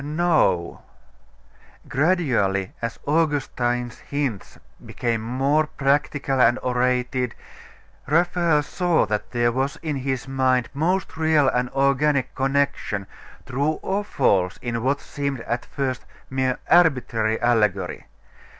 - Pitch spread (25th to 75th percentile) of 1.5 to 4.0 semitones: Yes, average, 3.5 semitones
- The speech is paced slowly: Yes, slow, 110 wpm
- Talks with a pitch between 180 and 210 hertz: No, low, 135 Hz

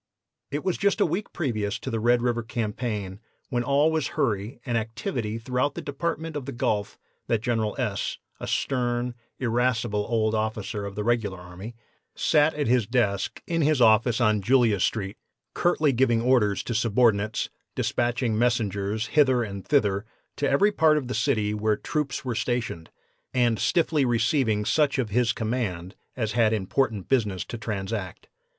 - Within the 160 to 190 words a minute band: Yes, average, 165 wpm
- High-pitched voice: No, low, 120 Hz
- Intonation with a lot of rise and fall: No, average, 3.7 semitones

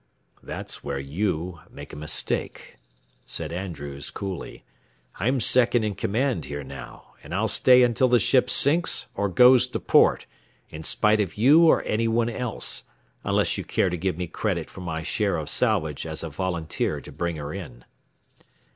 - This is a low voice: Yes, very low, 95 Hz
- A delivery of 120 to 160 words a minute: No, average, 170 wpm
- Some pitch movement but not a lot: No, wide, 6.6 semitones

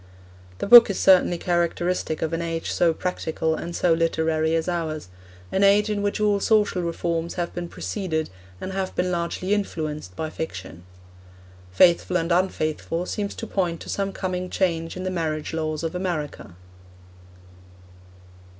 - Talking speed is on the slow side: No, average, 155 wpm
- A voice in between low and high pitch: Yes, medium, 170 Hz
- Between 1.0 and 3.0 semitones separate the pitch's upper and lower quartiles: Yes, narrow, 2.5 semitones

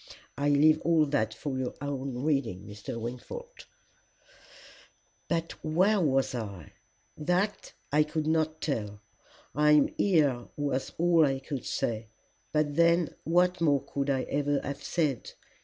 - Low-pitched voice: No, medium, 145 Hz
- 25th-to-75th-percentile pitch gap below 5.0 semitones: Yes, average, 3.7 semitones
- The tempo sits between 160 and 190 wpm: No, average, 140 wpm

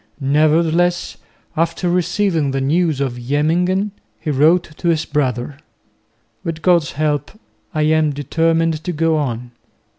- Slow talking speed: Yes, slow, 125 wpm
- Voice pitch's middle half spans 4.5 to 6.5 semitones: No, average, 2.8 semitones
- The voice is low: No, medium, 155 Hz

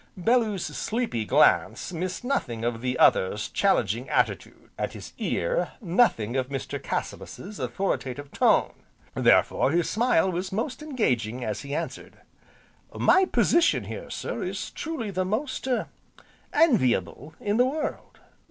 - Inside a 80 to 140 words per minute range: Yes, slow, 135 wpm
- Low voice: No, medium, 185 Hz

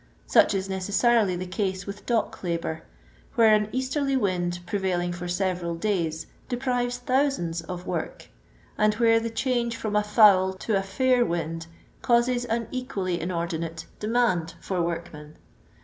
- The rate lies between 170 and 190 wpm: No, average, 150 wpm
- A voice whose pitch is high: Yes, high, 195 Hz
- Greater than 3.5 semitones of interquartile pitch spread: Yes, average, 5.2 semitones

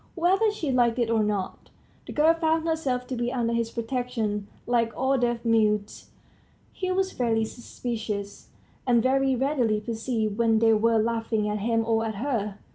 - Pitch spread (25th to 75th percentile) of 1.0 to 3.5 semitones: Yes, average, 2.8 semitones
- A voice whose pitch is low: No, high, 235 Hz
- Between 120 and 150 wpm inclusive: No, average, 170 wpm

